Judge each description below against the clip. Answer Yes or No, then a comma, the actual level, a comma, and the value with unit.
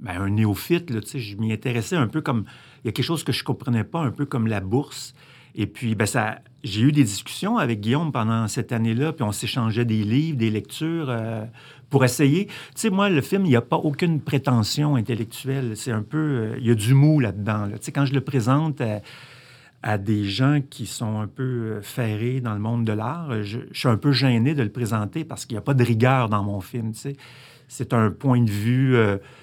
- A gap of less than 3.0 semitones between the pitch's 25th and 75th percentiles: No, average, 4.0 semitones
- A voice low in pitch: Yes, low, 125 Hz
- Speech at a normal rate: No, fast, 245 wpm